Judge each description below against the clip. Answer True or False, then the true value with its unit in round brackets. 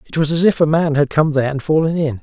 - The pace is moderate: False (325 wpm)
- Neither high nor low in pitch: True (150 Hz)